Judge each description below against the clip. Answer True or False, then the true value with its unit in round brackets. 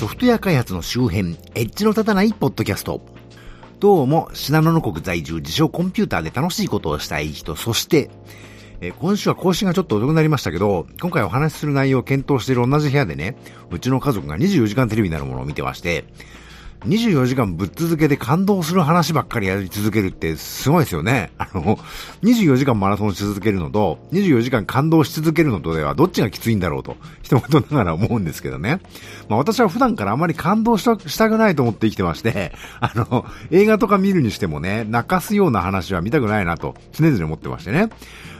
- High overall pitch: False (125 Hz)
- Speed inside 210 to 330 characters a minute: False (420 characters per minute)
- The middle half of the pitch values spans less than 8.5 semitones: False (9.0 semitones)